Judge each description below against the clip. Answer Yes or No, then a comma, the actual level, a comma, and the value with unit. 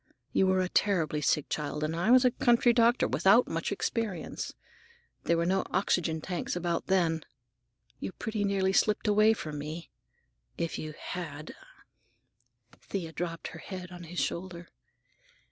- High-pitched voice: No, medium, 180 Hz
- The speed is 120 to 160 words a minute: Yes, average, 150 wpm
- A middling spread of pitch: Yes, average, 3.5 semitones